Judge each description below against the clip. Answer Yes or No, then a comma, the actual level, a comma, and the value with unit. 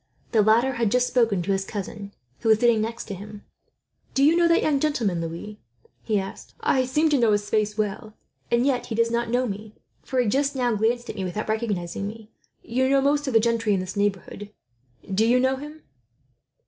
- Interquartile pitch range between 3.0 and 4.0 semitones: Yes, average, 3.6 semitones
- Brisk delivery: Yes, fast, 215 wpm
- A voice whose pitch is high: Yes, high, 225 Hz